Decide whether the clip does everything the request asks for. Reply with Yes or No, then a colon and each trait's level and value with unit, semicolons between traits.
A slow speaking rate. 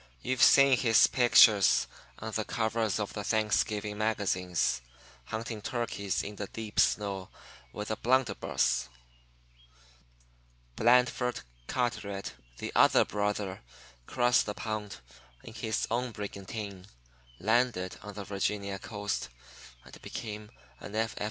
Yes: slow, 115 wpm